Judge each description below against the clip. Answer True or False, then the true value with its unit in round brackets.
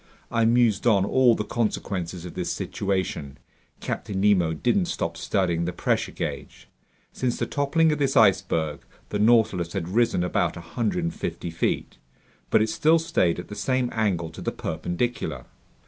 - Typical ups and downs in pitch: False (5.7 semitones)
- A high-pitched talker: False (105 Hz)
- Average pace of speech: True (155 wpm)